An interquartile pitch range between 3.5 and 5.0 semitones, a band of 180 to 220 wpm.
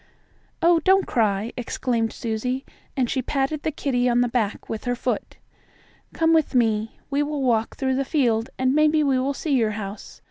Yes: average, 3.9 semitones; average, 185 wpm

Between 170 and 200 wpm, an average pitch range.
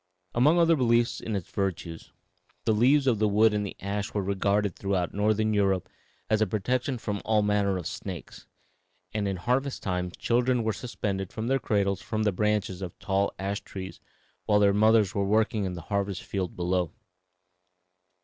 No: average, 175 wpm; narrow, 2.3 semitones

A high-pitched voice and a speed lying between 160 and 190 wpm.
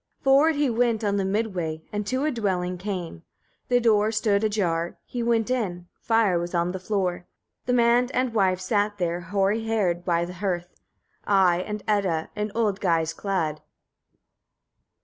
Yes: high, 200 Hz; average, 170 wpm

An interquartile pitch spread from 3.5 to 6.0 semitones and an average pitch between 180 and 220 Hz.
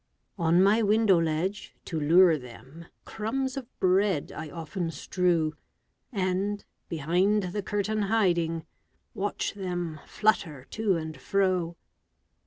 Yes: average, 3.9 semitones; medium, 185 Hz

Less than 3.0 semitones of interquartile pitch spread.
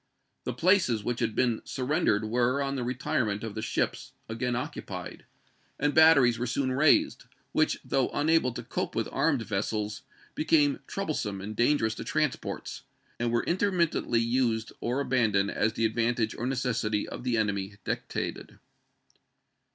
No: average, 3.9 semitones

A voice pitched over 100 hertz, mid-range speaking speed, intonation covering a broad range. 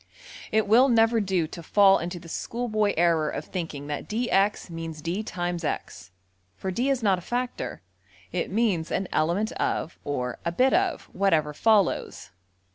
No: high, 190 Hz; average, 160 wpm; average, 5.0 semitones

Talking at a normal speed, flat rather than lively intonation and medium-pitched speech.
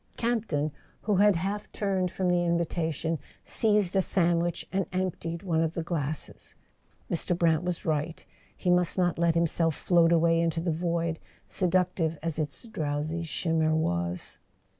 Yes: average, 150 wpm; narrow, 2.0 semitones; medium, 170 Hz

